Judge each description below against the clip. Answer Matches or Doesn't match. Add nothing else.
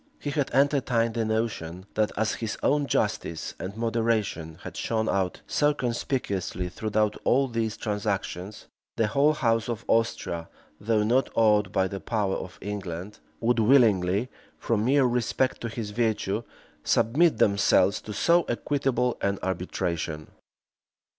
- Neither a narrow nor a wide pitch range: Matches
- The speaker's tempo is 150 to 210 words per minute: Doesn't match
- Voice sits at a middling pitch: Doesn't match